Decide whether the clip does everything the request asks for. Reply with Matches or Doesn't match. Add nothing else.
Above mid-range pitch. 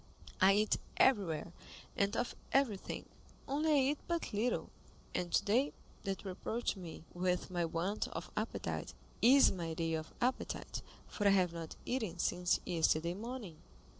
Matches